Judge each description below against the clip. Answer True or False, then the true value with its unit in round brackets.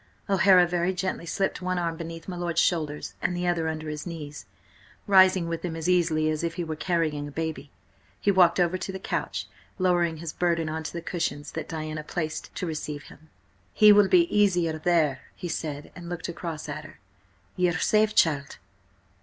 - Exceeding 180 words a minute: True (200 wpm)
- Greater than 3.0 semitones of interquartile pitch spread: False (2.4 semitones)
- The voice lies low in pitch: False (170 Hz)